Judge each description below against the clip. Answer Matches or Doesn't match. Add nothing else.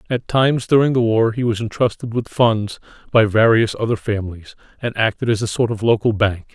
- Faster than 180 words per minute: Matches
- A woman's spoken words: Doesn't match